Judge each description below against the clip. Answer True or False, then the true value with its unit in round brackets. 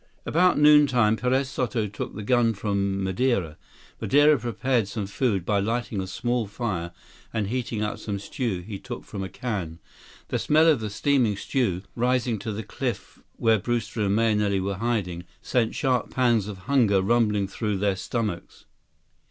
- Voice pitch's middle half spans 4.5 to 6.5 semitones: False (3.8 semitones)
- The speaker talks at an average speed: True (165 wpm)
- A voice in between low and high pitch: False (110 Hz)